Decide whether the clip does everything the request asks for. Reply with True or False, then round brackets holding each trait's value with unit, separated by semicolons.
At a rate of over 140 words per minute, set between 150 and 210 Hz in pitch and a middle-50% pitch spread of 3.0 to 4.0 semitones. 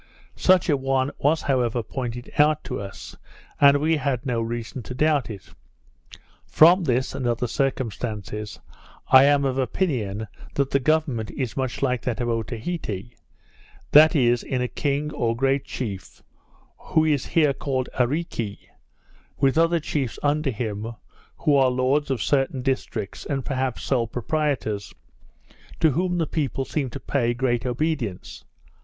False (150 wpm; 130 Hz; 3.6 semitones)